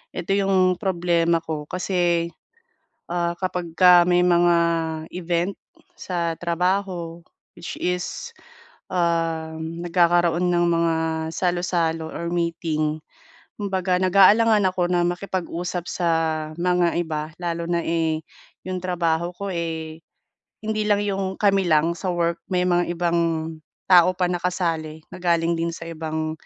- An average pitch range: No, narrow, 1.5 semitones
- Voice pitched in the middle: Yes, medium, 175 Hz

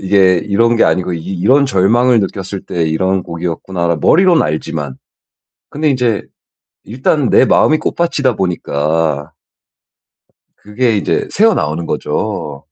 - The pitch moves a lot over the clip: Yes, wide, 6.9 semitones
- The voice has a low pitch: Yes, very low, 95 Hz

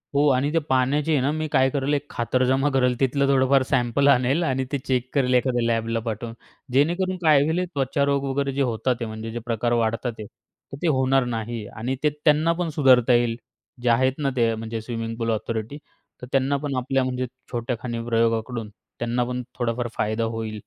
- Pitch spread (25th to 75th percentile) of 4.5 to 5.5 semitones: No, average, 3.1 semitones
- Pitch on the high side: No, low, 125 Hz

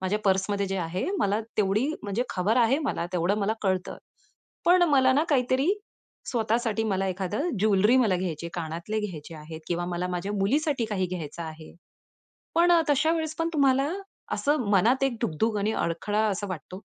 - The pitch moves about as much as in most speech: No, wide, 6.0 semitones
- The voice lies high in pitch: Yes, high, 205 Hz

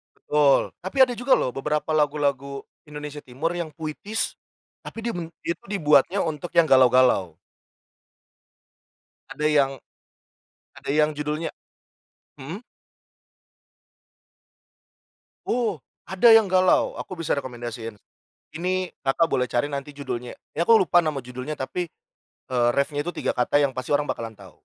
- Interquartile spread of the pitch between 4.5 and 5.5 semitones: Yes, average, 4.8 semitones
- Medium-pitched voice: Yes, medium, 150 Hz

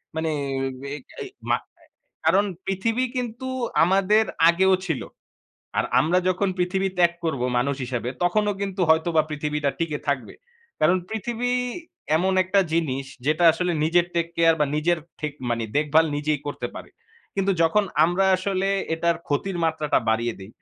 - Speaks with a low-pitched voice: No, medium, 170 Hz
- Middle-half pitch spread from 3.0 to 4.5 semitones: Yes, average, 4.2 semitones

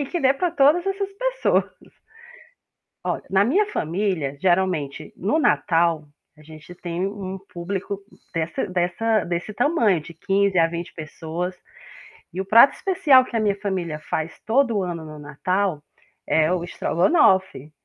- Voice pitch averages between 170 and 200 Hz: Yes, medium, 185 Hz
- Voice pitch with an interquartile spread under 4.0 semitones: No, average, 5.2 semitones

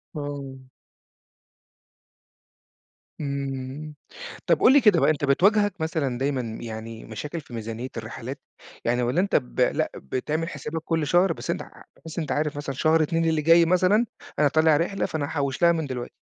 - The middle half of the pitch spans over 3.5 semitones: Yes, average, 4.0 semitones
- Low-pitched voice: No, medium, 150 Hz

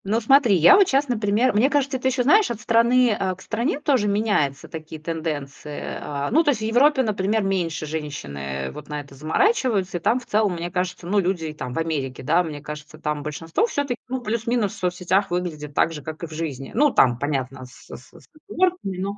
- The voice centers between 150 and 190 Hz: Yes, medium, 185 Hz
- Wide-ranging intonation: Yes, wide, 7.6 semitones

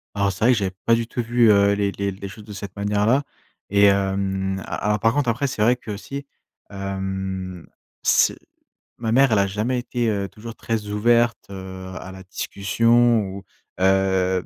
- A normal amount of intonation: Yes, average, 3.1 semitones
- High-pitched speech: No, low, 100 Hz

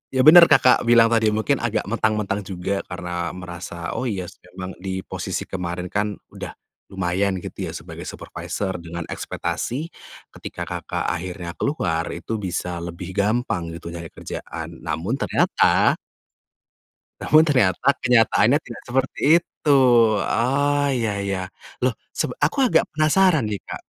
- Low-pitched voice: Yes, low, 100 Hz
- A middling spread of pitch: No, wide, 6.0 semitones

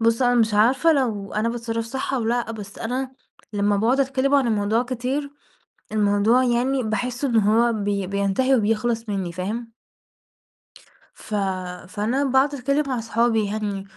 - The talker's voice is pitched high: Yes, high, 230 Hz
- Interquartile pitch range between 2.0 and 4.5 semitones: Yes, average, 3.4 semitones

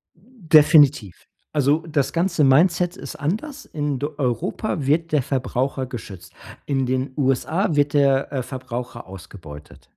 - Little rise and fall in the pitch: No, average, 3.7 semitones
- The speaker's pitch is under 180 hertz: Yes, medium, 140 Hz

